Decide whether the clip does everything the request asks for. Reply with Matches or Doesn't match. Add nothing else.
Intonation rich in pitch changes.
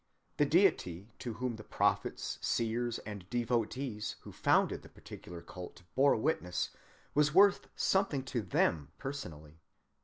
Matches